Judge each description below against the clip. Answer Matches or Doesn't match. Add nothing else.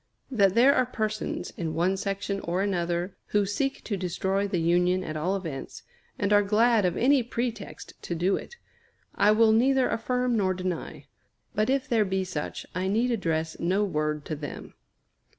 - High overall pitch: Matches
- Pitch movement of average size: Matches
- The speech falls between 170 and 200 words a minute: Matches